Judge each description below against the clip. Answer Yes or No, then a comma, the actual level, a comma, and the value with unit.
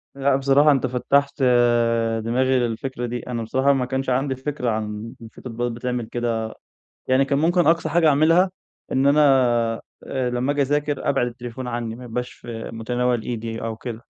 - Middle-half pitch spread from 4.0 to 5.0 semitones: No, average, 2.9 semitones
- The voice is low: Yes, low, 125 Hz